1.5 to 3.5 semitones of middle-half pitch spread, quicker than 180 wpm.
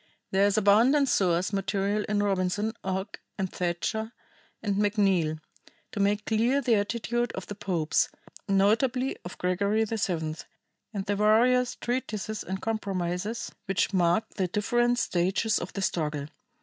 No: average, 3.0 semitones; slow, 135 wpm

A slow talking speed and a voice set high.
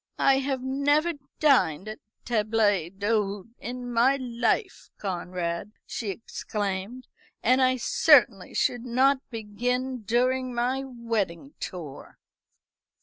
Yes: slow, 110 wpm; high, 235 Hz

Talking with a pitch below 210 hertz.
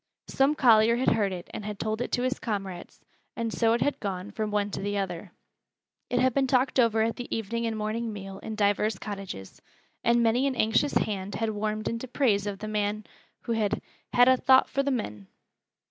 No: high, 220 Hz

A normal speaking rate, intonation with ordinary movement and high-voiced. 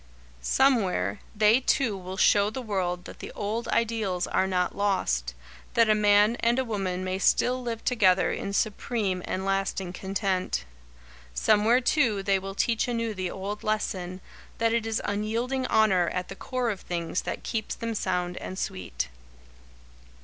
Yes: average, 160 wpm; average, 3.6 semitones; high, 205 Hz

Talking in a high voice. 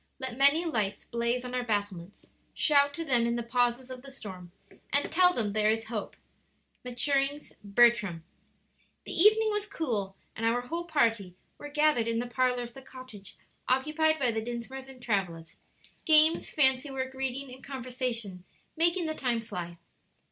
Yes: very high, 250 Hz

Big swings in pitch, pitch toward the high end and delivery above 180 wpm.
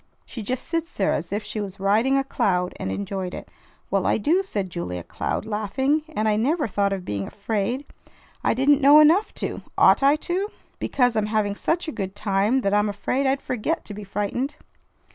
Yes: wide, 5.8 semitones; high, 215 Hz; average, 200 wpm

